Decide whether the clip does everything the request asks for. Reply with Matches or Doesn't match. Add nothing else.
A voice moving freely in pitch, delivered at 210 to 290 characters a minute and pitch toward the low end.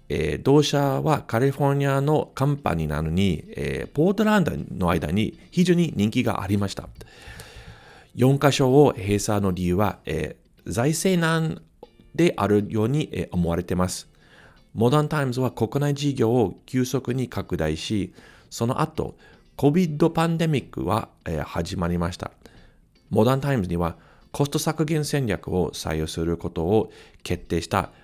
Matches